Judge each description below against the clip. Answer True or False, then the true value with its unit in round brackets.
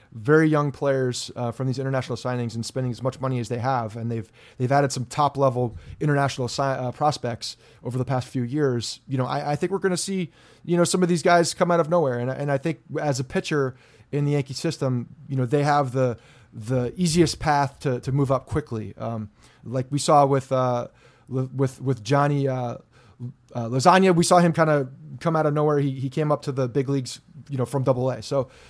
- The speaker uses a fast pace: True (230 wpm)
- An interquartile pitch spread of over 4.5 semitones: False (2.9 semitones)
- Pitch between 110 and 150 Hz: True (135 Hz)